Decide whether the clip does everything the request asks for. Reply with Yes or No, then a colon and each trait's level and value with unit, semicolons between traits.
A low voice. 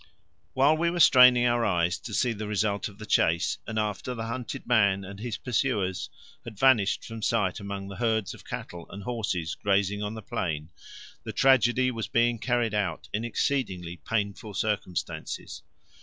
Yes: low, 110 Hz